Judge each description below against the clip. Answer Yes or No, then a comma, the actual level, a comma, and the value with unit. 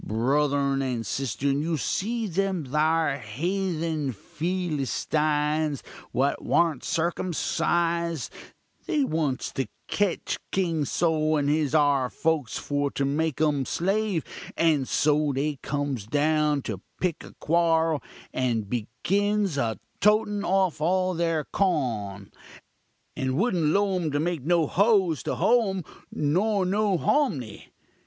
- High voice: No, medium, 155 Hz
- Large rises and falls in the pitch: No, average, 4.5 semitones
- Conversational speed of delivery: No, slow, 125 wpm